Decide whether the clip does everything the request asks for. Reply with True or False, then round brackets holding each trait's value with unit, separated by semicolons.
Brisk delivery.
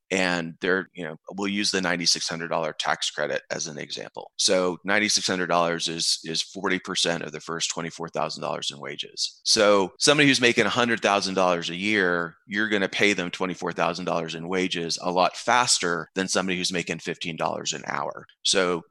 False (160 wpm)